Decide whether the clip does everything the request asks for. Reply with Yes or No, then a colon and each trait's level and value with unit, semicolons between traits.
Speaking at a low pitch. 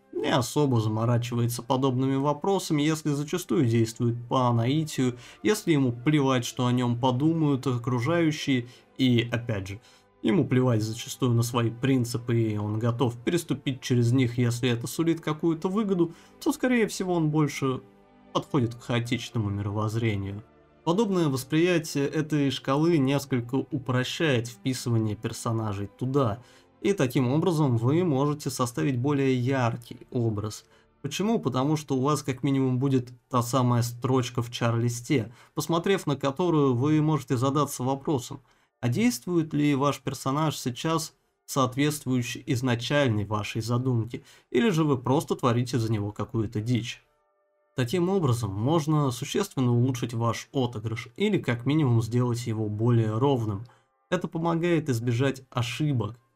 Yes: low, 130 Hz